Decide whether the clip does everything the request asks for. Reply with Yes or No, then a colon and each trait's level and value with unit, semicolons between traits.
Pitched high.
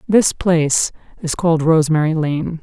No: medium, 160 Hz